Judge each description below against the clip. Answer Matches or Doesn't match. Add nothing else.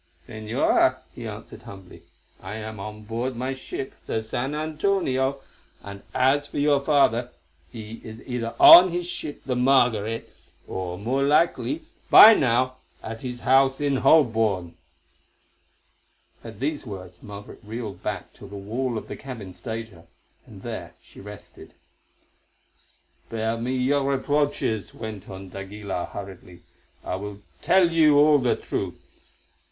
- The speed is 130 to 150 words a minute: Matches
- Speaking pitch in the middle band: Doesn't match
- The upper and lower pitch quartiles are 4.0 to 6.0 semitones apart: Matches